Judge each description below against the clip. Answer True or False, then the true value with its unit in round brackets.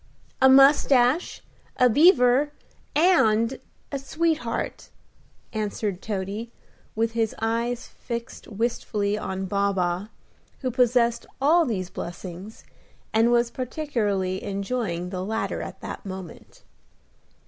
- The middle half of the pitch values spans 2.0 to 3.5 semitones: False (4.1 semitones)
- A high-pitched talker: True (230 Hz)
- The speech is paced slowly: True (105 wpm)